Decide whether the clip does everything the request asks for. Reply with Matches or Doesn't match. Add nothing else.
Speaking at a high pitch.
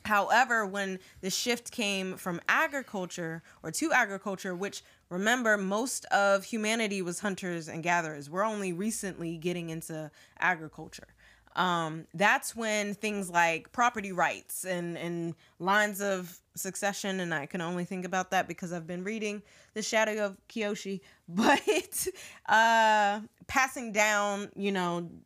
Matches